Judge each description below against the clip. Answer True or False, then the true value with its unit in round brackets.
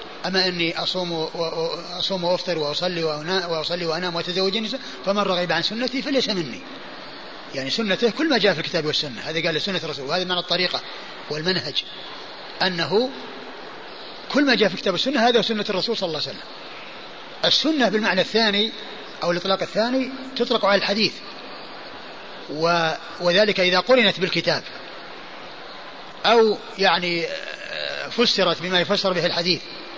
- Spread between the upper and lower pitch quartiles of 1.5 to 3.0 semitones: False (4.4 semitones)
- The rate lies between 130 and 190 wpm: True (135 wpm)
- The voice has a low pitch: False (185 Hz)